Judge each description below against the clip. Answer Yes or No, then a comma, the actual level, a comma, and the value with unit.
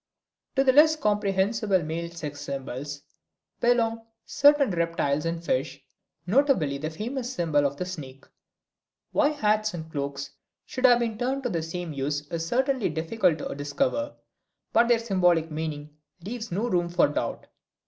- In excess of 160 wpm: No, average, 150 wpm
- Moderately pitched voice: Yes, medium, 175 Hz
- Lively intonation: Yes, wide, 7.8 semitones